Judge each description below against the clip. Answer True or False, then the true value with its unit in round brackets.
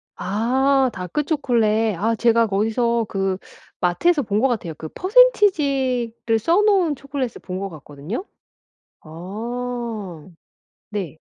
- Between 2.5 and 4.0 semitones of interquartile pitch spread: False (5.6 semitones)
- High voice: True (230 Hz)